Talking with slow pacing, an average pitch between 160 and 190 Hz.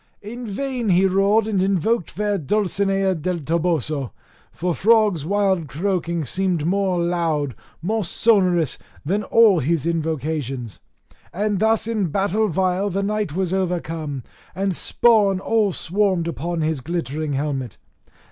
Yes: slow, 130 wpm; medium, 185 Hz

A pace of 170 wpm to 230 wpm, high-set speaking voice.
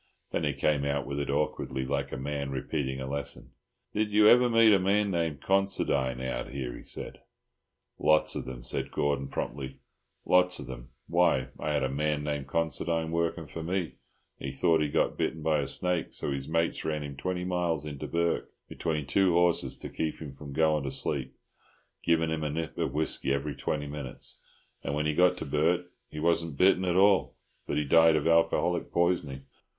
No: average, 195 wpm; very low, 75 Hz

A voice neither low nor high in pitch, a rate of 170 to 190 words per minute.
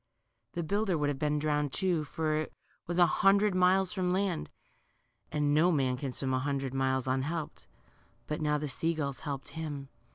Yes: medium, 150 Hz; average, 185 wpm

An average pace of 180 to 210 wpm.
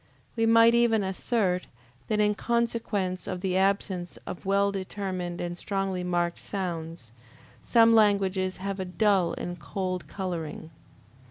No: slow, 135 wpm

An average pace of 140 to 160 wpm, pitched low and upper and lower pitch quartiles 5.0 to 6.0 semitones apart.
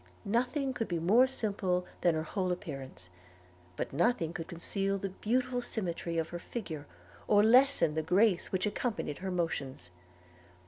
No: average, 150 wpm; medium, 185 Hz; wide, 5.4 semitones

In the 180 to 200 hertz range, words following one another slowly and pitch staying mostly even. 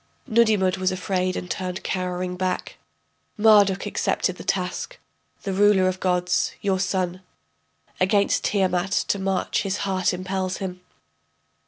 Yes: medium, 185 Hz; slow, 130 wpm; narrow, 1.3 semitones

